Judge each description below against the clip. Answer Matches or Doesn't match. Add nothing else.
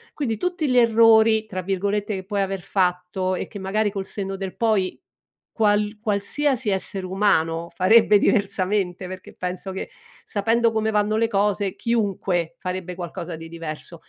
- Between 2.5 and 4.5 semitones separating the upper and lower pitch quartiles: Matches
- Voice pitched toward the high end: Matches